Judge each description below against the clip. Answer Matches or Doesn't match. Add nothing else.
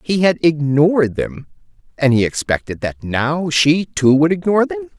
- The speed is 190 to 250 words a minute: Doesn't match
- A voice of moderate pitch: Matches